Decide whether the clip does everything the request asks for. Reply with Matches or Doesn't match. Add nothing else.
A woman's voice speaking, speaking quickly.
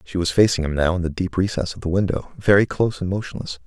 Doesn't match